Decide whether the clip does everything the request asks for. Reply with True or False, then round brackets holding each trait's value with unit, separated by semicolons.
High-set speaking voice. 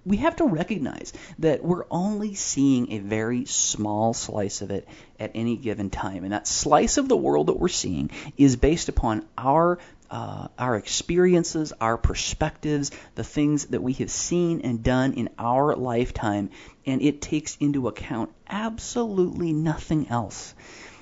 False (135 Hz)